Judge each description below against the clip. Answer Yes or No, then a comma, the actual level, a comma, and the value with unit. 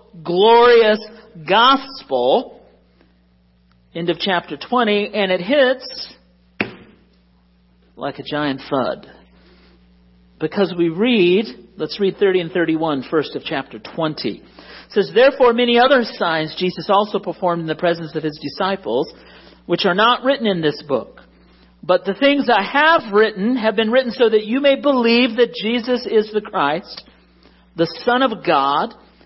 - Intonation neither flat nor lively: No, wide, 7.8 semitones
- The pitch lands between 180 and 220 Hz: Yes, medium, 185 Hz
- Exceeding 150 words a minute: No, average, 145 wpm